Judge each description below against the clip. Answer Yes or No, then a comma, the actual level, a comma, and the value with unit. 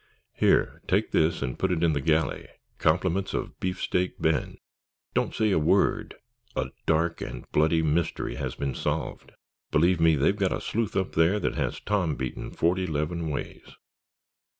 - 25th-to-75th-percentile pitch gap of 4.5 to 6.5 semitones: No, average, 2.9 semitones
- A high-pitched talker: No, very low, 80 Hz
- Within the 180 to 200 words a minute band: No, average, 165 wpm